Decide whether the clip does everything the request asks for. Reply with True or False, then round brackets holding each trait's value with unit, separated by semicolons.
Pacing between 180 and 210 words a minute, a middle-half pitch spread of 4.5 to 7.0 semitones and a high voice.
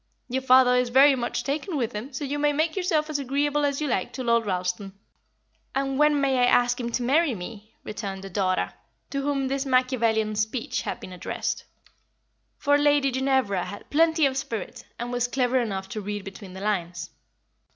True (195 wpm; 4.8 semitones; 255 Hz)